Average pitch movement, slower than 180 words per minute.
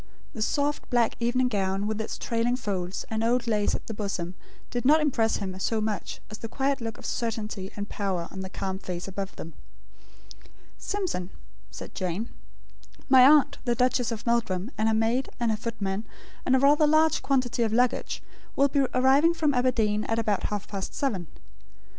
No: average, 4.0 semitones; average, 185 wpm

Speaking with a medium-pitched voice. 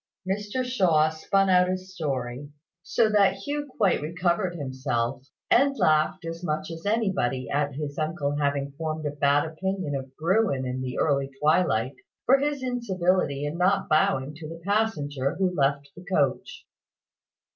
Yes: medium, 160 Hz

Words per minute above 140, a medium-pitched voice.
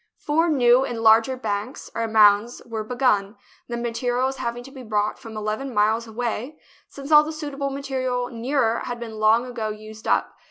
No: average, 175 wpm; high, 240 Hz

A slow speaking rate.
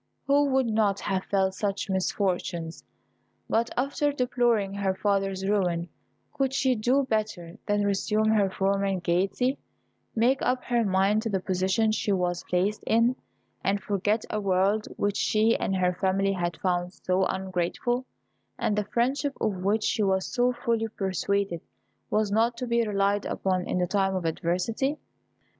No: average, 155 wpm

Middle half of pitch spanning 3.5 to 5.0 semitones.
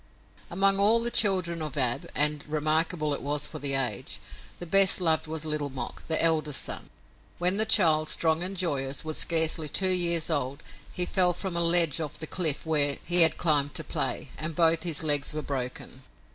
No: average, 3.0 semitones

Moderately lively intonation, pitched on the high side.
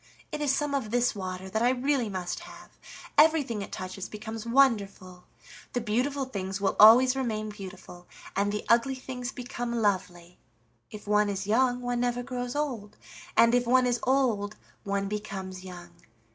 Yes: average, 4.1 semitones; high, 225 Hz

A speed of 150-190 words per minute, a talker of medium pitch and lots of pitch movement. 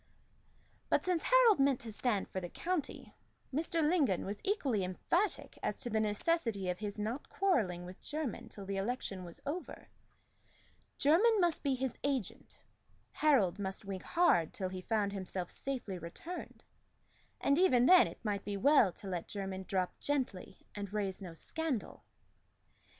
No: average, 155 wpm; high, 220 Hz; wide, 7.8 semitones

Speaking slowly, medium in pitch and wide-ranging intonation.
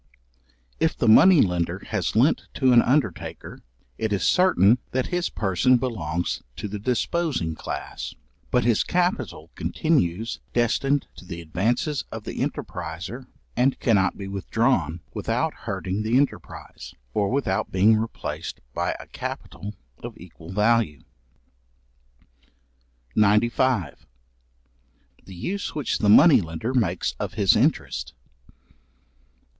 No: slow, 120 wpm; low, 110 Hz; wide, 5.8 semitones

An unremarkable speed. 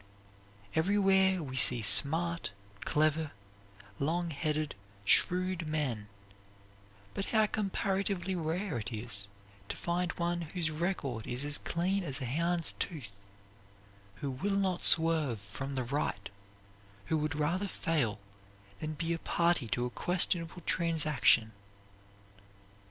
No: slow, 120 wpm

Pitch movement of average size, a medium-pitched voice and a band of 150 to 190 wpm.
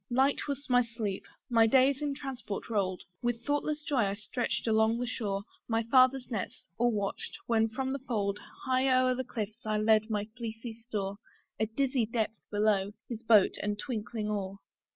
No: average, 3.3 semitones; high, 230 Hz; average, 175 wpm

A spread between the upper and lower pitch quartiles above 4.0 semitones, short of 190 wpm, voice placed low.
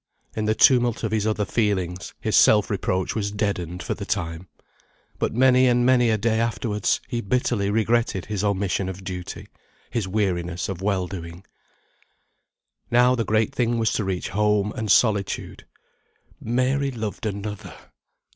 No: average, 3.2 semitones; average, 155 wpm; low, 105 Hz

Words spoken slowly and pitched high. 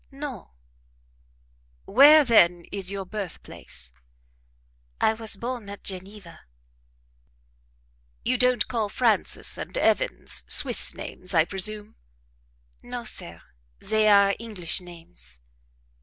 Yes: slow, 100 wpm; high, 205 Hz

